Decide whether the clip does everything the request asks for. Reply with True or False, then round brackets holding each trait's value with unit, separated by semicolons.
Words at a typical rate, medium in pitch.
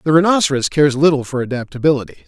True (160 wpm; 145 Hz)